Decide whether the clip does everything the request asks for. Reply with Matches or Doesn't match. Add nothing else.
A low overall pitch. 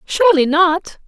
Doesn't match